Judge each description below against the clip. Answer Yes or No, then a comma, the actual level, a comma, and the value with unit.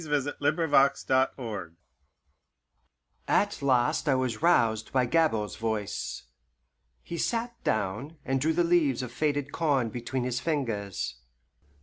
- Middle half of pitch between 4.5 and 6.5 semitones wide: Yes, average, 5.1 semitones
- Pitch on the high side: No, low, 130 Hz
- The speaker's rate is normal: No, slow, 130 wpm